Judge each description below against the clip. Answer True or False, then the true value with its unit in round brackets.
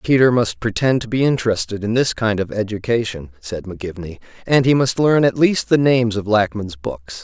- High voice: False (110 Hz)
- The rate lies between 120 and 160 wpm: False (200 wpm)